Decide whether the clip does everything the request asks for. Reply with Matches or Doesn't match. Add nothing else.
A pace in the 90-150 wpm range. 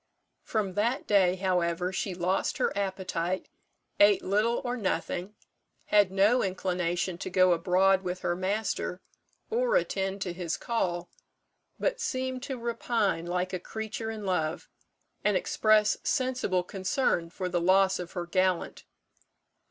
Matches